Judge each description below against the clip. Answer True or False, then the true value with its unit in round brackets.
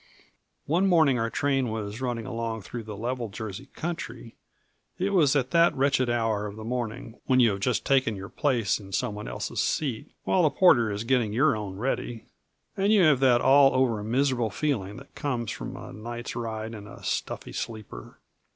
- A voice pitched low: True (120 Hz)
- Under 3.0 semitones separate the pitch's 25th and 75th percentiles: False (3.8 semitones)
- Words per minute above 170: True (190 wpm)